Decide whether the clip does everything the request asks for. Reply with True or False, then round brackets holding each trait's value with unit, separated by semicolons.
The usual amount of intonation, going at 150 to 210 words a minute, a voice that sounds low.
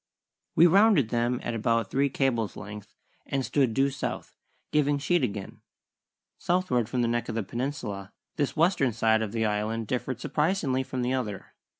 True (4.0 semitones; 170 wpm; 125 Hz)